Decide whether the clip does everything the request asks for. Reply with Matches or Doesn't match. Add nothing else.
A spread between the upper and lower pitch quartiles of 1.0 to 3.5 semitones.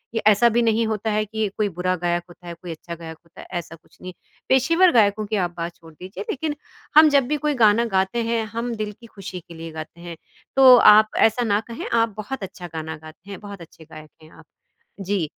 Doesn't match